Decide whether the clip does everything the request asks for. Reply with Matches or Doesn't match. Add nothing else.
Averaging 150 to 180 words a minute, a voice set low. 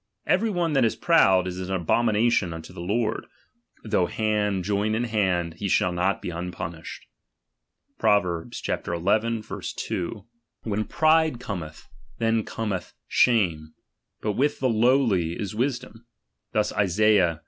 Doesn't match